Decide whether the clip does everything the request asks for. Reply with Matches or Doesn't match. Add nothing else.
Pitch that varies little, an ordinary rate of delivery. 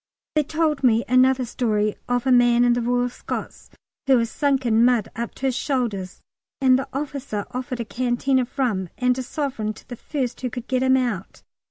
Doesn't match